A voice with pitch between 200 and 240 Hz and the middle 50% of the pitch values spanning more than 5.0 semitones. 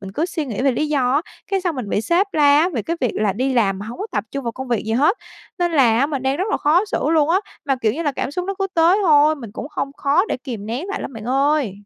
No: very high, 280 Hz; wide, 5.5 semitones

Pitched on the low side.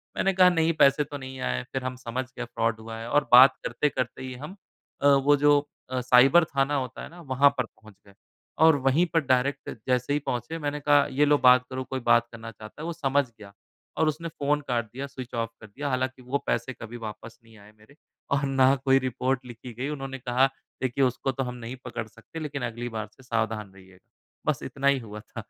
Yes: low, 130 Hz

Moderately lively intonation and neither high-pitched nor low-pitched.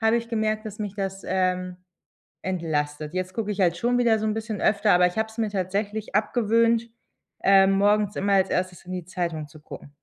No: average, 3.1 semitones; high, 195 Hz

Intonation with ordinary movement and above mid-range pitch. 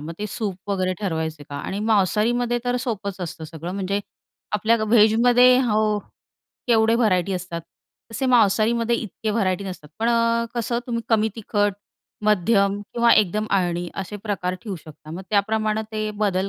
Yes: average, 3.6 semitones; high, 210 Hz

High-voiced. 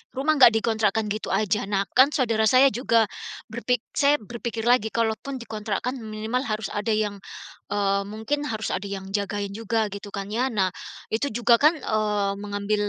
Yes: high, 220 Hz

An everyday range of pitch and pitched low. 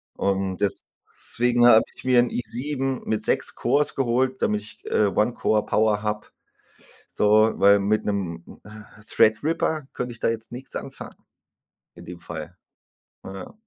Yes: average, 3.4 semitones; low, 110 Hz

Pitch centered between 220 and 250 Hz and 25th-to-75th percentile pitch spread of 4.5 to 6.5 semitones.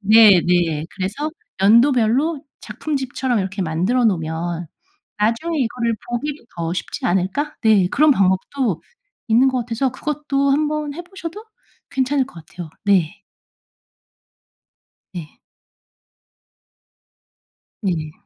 No: high, 230 Hz; wide, 7.2 semitones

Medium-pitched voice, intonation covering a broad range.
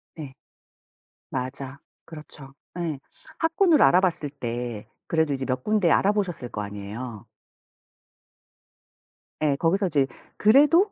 Yes: medium, 150 Hz; wide, 7.0 semitones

